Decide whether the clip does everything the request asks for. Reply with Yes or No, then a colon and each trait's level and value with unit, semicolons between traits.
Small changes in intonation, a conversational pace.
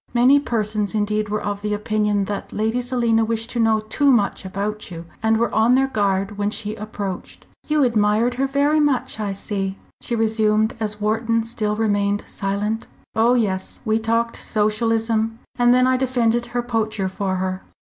Yes: narrow, 2.2 semitones; average, 170 wpm